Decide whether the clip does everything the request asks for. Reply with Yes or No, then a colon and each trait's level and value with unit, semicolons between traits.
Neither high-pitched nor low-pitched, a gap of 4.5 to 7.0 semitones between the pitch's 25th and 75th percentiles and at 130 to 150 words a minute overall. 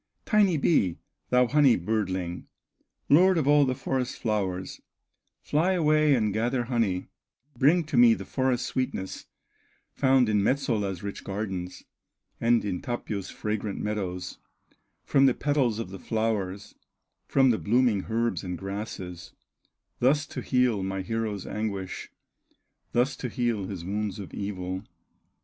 No: low, 110 Hz; average, 5.0 semitones; slow, 135 wpm